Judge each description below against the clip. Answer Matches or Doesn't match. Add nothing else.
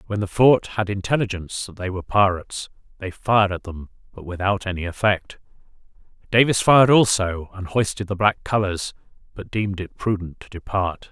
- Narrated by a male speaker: Matches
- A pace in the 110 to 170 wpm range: Matches